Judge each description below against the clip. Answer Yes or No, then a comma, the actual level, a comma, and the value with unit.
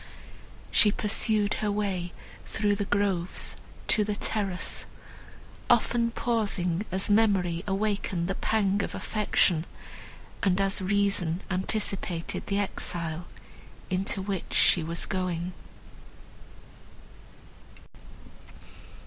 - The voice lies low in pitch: No, high, 195 Hz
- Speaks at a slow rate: Yes, slow, 95 wpm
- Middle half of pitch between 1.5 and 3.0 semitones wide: Yes, narrow, 2.5 semitones